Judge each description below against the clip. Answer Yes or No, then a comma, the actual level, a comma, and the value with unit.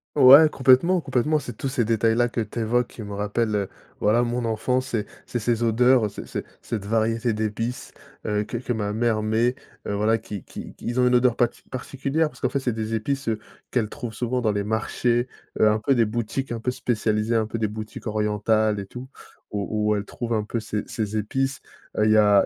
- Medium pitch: No, low, 115 Hz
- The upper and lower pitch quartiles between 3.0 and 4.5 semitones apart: No, narrow, 2.6 semitones